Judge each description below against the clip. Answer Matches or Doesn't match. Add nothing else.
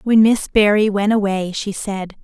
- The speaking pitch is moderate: Doesn't match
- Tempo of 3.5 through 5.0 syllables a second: Matches